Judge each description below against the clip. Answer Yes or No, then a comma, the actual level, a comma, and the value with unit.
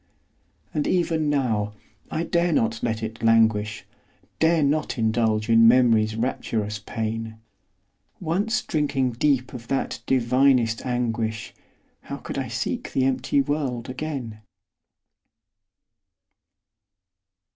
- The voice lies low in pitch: Yes, low, 120 Hz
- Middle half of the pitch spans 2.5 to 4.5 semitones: Yes, average, 4.1 semitones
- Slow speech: Yes, slow, 105 wpm